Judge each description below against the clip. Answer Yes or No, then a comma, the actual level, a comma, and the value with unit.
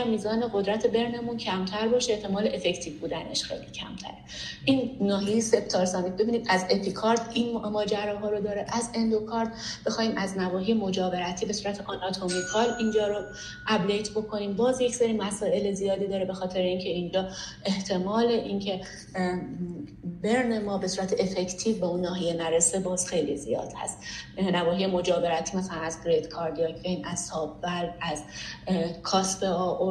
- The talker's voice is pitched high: Yes, high, 195 Hz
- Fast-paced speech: No, average, 140 wpm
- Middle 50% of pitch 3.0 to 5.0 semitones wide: Yes, average, 3.3 semitones